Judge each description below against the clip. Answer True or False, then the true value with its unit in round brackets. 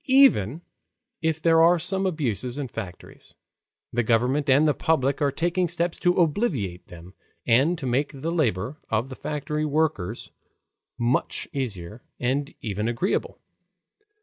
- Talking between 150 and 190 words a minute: False (140 wpm)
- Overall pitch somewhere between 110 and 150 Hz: True (140 Hz)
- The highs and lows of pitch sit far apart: True (5.7 semitones)